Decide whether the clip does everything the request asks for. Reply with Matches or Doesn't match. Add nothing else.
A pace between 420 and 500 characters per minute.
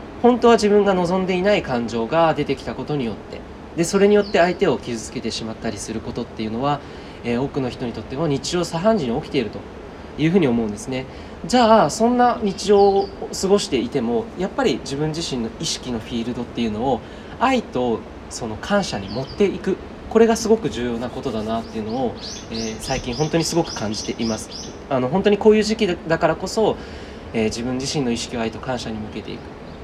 Matches